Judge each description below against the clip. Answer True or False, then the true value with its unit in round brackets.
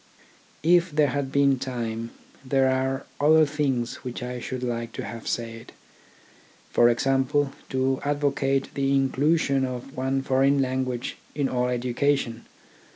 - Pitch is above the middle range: False (135 Hz)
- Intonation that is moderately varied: False (2.2 semitones)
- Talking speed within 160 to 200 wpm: False (135 wpm)